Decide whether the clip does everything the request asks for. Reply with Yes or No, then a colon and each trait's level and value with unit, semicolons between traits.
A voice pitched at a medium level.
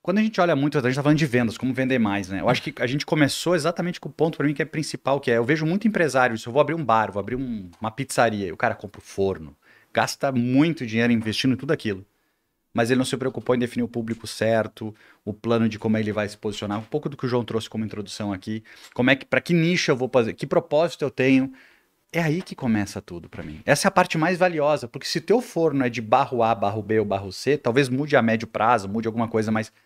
No: low, 125 Hz